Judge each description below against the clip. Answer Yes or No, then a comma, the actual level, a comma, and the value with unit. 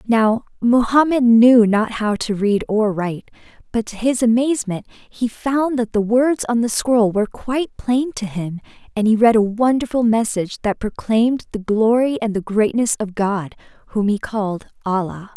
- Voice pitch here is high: Yes, high, 225 Hz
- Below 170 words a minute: No, average, 175 wpm